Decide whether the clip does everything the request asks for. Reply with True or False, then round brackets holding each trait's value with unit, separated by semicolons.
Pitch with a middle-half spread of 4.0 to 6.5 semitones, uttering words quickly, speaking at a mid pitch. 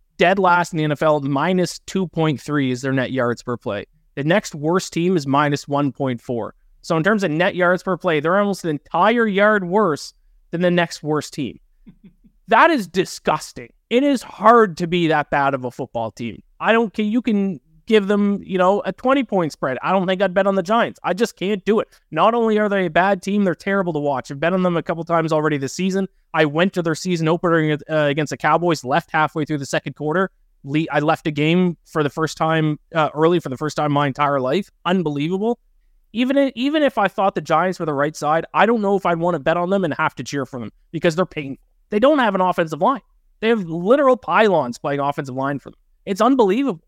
True (4.7 semitones; 235 wpm; 175 Hz)